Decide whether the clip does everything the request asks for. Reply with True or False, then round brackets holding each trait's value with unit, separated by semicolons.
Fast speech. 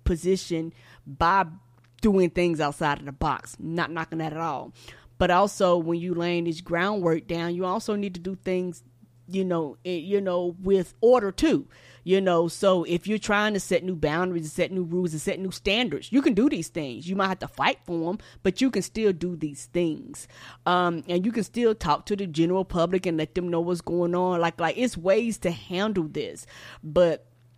True (210 wpm)